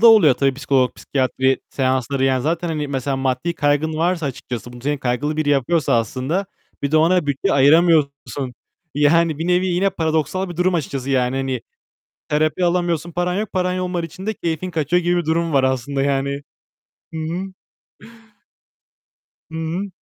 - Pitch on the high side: No, medium, 155 Hz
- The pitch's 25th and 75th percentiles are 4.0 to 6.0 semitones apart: Yes, average, 4.3 semitones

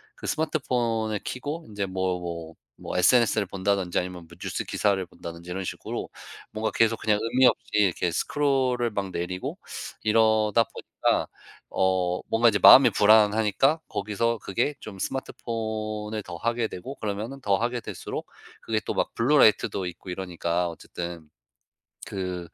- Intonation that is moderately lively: Yes, average, 4.0 semitones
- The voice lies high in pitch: No, low, 105 Hz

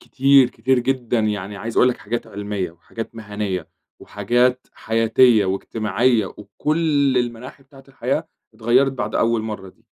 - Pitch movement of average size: Yes, average, 3.7 semitones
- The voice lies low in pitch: Yes, low, 115 Hz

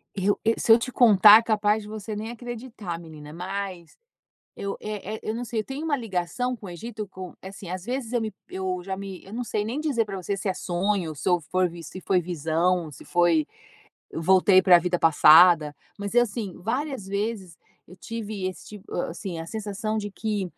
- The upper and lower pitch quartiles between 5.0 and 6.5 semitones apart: No, average, 3.7 semitones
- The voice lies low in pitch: No, high, 200 Hz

